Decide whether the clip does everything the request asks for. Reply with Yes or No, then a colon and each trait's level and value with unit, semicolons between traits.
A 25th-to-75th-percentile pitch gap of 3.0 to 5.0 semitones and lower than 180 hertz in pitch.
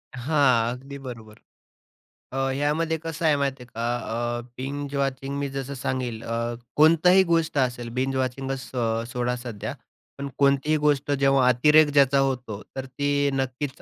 No: narrow, 2.4 semitones; low, 135 Hz